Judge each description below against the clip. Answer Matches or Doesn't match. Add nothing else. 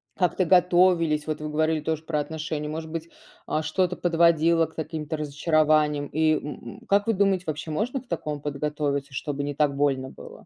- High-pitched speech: Doesn't match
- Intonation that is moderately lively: Doesn't match